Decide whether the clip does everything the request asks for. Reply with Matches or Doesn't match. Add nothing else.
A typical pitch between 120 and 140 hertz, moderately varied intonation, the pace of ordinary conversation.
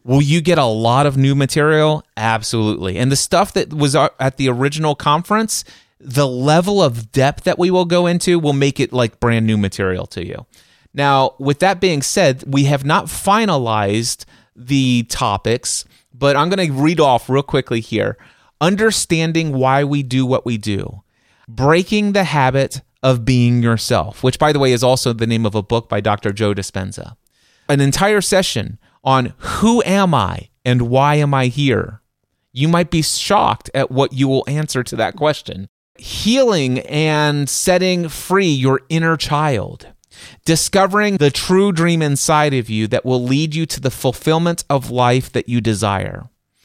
Matches